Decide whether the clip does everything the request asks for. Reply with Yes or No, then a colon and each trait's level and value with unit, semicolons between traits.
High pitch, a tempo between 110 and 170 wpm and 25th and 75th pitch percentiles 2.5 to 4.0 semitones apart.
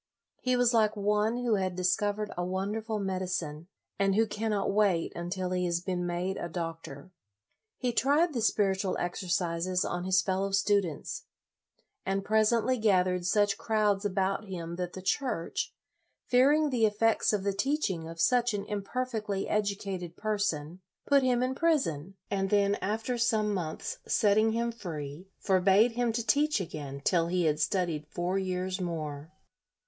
Yes: high, 195 Hz; average, 160 wpm; average, 3.6 semitones